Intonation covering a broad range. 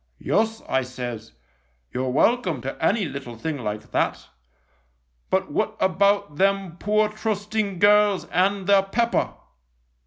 Yes: wide, 8.0 semitones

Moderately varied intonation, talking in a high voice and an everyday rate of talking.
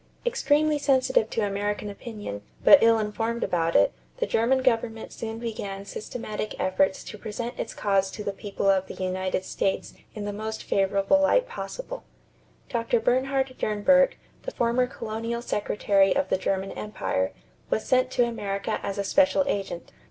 Yes: average, 4.2 semitones; high, 220 Hz; average, 160 wpm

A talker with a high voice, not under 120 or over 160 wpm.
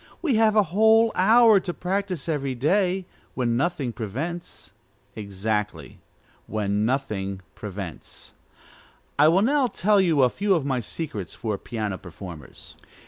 No: medium, 140 Hz; slow, 135 wpm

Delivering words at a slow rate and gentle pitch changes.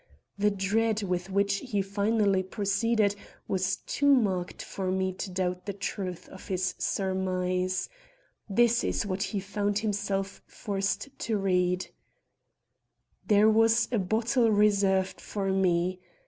Yes: slow, 130 wpm; narrow, 2.0 semitones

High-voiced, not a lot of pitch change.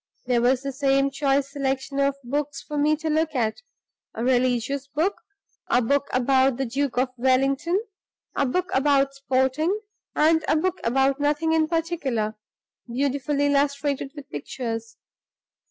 Yes: very high, 275 Hz; narrow, 2.3 semitones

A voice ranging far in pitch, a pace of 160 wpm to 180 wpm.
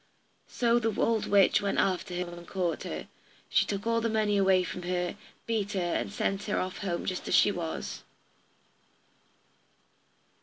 No: average, 2.9 semitones; average, 165 wpm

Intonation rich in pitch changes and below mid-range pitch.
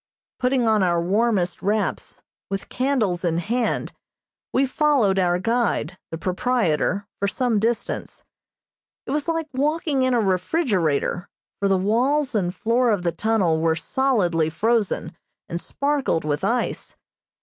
No: wide, 6.0 semitones; high, 210 Hz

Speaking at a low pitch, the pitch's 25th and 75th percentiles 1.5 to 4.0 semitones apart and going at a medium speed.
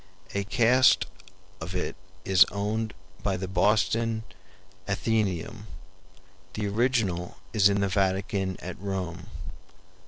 No: low, 100 Hz; average, 2.8 semitones; slow, 105 wpm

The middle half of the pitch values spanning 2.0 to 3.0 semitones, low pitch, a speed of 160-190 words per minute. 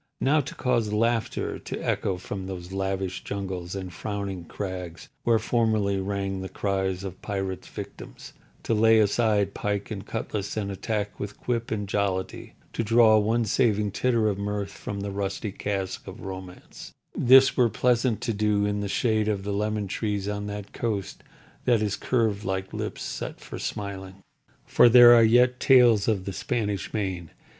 Yes: narrow, 2.5 semitones; low, 100 Hz; average, 165 wpm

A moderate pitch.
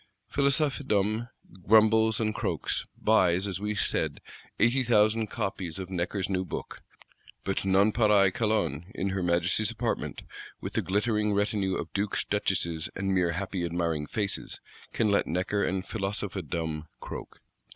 No: low, 100 Hz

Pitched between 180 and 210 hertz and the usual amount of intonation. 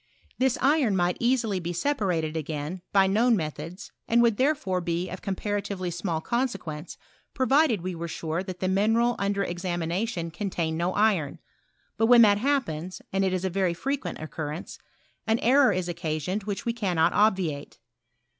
Yes: high, 190 Hz; average, 4.7 semitones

